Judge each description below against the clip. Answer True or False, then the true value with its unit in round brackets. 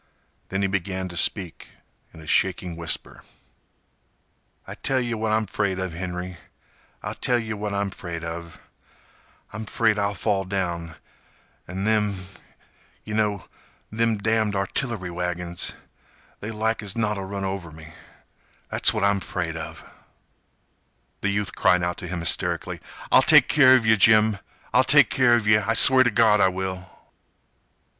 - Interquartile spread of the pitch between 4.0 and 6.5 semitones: False (3.4 semitones)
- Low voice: True (100 Hz)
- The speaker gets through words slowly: False (150 wpm)